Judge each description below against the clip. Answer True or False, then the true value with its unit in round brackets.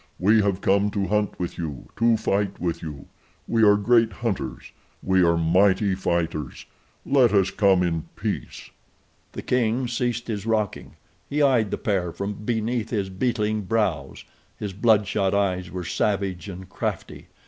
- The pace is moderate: True (155 wpm)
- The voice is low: True (100 Hz)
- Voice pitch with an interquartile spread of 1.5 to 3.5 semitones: True (3.2 semitones)